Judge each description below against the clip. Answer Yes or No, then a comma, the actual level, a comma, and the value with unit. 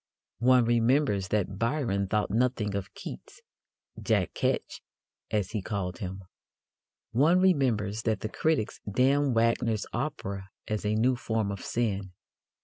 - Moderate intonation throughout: Yes, average, 4.0 semitones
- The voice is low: Yes, low, 110 Hz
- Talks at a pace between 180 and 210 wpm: No, slow, 135 wpm